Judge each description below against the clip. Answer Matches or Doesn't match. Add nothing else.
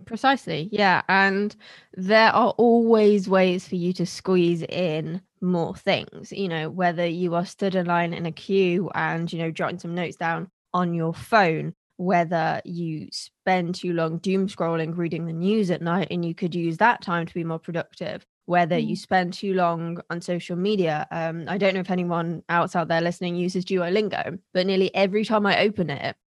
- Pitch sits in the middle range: Matches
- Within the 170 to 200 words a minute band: Matches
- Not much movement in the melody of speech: Matches